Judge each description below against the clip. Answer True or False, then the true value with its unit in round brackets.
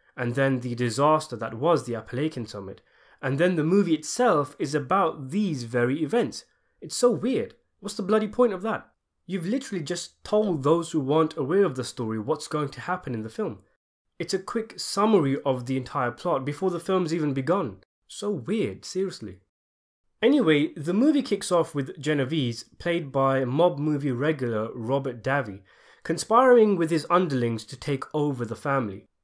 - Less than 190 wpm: True (175 wpm)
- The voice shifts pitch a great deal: True (6.3 semitones)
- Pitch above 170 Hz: False (155 Hz)